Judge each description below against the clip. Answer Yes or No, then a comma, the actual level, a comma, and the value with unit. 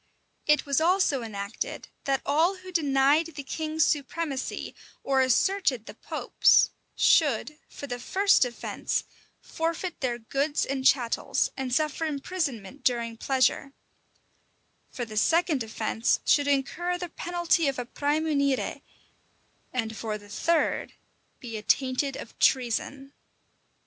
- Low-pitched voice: No, very high, 275 Hz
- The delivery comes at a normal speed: No, slow, 125 wpm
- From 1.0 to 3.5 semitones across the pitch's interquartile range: No, average, 4.4 semitones